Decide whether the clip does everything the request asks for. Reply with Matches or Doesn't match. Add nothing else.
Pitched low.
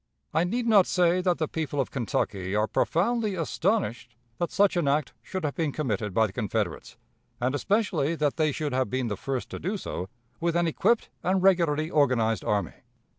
Doesn't match